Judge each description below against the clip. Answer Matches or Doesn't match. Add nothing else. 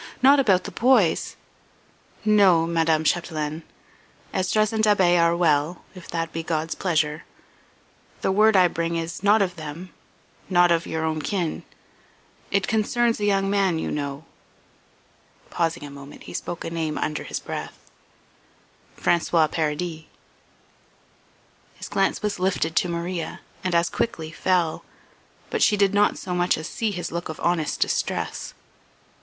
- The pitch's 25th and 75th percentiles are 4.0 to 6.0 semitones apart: Doesn't match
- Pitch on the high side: Doesn't match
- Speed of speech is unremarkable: Matches